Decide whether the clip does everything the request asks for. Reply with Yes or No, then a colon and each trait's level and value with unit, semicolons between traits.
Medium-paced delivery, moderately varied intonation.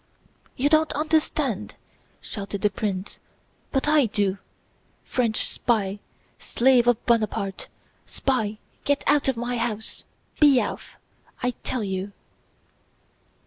No: slow, 110 wpm; average, 4.6 semitones